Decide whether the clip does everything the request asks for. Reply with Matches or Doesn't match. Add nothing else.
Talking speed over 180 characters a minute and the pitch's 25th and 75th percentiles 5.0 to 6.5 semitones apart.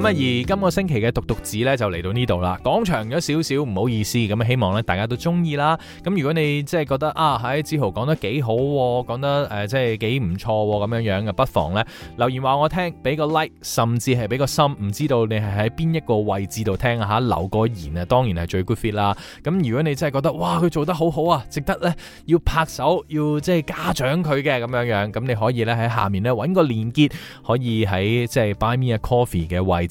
Matches